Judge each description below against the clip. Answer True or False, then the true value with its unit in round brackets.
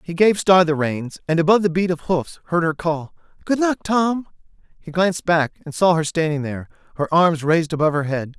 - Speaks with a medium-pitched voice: True (165 Hz)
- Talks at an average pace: False (220 wpm)